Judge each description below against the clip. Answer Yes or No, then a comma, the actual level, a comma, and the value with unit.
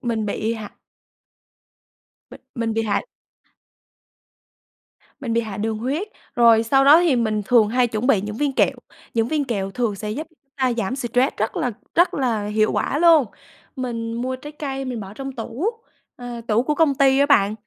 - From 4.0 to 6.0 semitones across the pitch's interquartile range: No, average, 3.6 semitones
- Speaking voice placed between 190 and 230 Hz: No, high, 240 Hz